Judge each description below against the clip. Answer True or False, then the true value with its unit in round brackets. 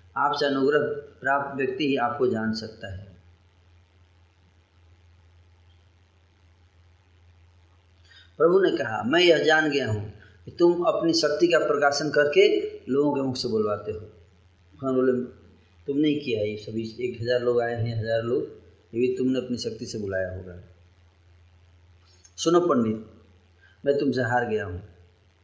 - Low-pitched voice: True (105 Hz)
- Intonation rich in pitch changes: True (6.9 semitones)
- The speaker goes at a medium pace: True (135 wpm)